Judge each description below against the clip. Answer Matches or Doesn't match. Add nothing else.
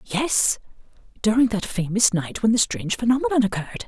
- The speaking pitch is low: Doesn't match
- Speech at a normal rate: Matches